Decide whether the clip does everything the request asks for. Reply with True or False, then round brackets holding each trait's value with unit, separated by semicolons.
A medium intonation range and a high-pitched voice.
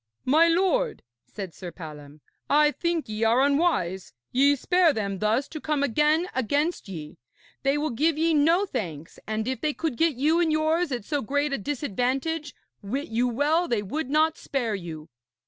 False (6.4 semitones; 280 Hz)